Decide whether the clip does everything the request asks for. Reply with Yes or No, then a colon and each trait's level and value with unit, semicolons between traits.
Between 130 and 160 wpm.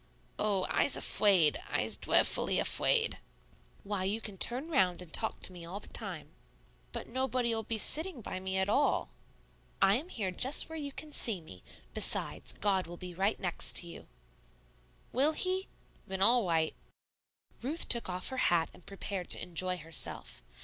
No: average, 170 wpm